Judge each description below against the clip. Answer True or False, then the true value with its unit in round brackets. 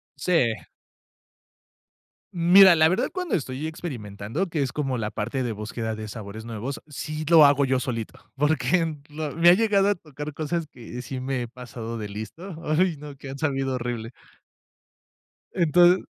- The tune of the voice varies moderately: False (5.7 semitones)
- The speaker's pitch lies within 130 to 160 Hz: True (140 Hz)